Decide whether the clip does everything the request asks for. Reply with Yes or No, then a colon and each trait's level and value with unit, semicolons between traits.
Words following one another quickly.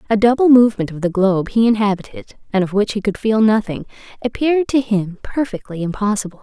No: average, 185 wpm